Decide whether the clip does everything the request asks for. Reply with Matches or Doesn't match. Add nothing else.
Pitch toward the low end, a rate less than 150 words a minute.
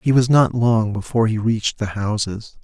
Doesn't match